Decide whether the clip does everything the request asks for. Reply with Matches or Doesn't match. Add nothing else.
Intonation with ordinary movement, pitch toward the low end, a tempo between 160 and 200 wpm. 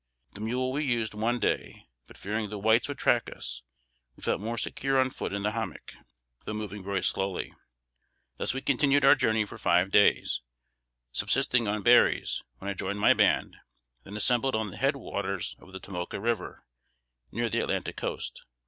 Matches